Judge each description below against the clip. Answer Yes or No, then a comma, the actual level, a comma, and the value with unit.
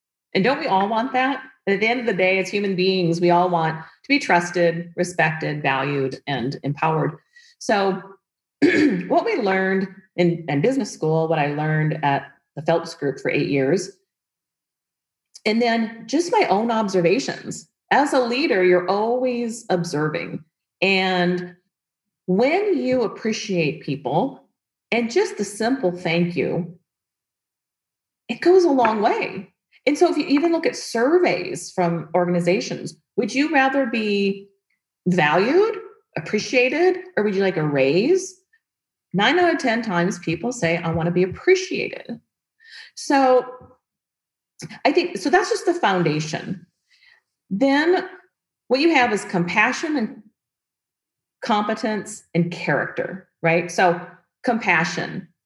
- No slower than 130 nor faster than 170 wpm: Yes, slow, 135 wpm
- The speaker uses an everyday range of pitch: No, wide, 7.2 semitones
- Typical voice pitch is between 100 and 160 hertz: No, high, 195 Hz